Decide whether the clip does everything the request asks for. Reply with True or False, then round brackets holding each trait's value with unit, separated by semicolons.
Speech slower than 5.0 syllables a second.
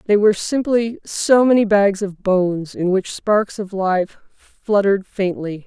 True (4.1 syllables/s)